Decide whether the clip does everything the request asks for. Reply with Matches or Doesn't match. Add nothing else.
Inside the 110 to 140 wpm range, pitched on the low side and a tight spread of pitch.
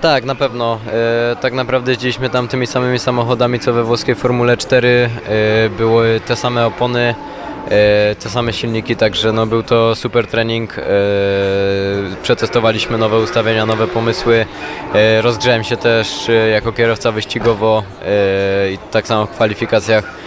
Doesn't match